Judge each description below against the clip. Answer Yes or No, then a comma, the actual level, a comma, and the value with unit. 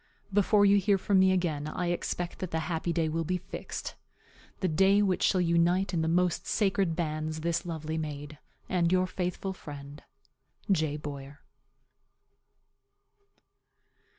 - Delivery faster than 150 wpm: No, average, 145 wpm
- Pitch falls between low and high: Yes, medium, 170 Hz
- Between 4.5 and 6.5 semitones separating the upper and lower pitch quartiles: No, average, 3.0 semitones